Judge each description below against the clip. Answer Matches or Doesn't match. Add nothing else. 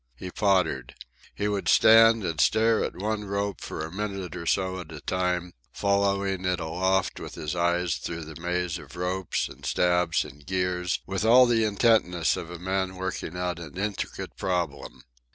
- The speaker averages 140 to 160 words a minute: Doesn't match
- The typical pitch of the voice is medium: Doesn't match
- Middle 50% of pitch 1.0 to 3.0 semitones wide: Matches